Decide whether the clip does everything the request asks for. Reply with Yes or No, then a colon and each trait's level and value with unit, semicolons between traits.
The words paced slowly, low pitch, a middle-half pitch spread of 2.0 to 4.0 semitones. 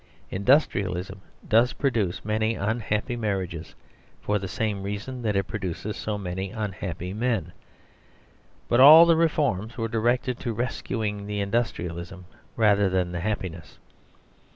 Yes: slow, 130 wpm; low, 105 Hz; average, 3.6 semitones